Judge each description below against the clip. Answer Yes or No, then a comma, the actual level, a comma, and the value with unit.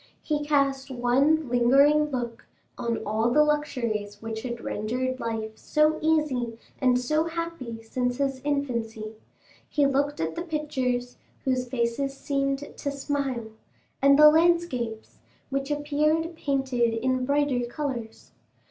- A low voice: No, very high, 265 Hz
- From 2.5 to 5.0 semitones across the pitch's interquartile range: Yes, average, 3.7 semitones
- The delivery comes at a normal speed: No, slow, 130 wpm